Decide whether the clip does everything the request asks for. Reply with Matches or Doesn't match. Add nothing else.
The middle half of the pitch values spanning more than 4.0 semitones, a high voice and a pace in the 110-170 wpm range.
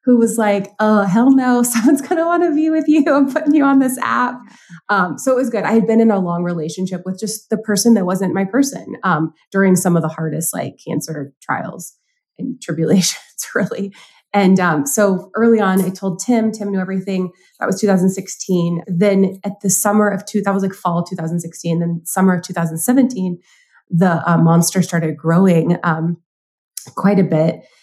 Doesn't match